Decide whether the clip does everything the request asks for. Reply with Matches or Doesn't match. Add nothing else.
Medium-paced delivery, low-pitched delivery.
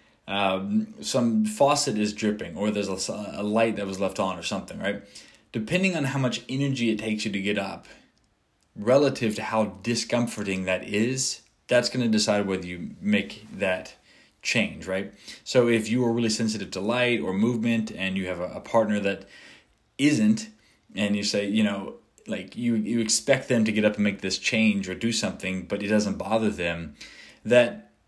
Matches